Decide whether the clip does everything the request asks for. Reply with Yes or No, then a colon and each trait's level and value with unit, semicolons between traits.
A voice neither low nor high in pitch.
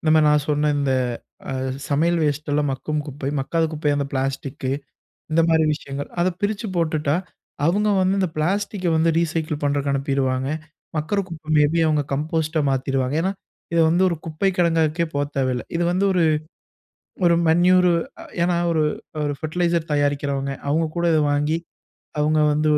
Yes: medium, 155 Hz